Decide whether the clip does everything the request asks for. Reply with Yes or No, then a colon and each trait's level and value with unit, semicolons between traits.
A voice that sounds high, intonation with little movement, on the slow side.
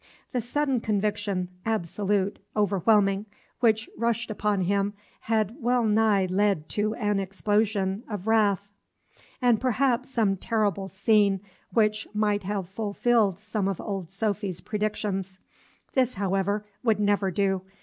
Yes: high, 205 Hz; narrow, 2.1 semitones; slow, 125 wpm